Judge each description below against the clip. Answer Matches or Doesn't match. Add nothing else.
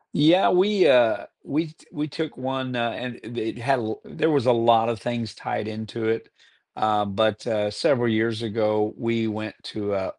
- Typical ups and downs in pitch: Matches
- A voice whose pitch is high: Doesn't match